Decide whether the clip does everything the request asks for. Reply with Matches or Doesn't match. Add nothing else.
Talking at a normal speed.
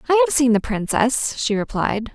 Matches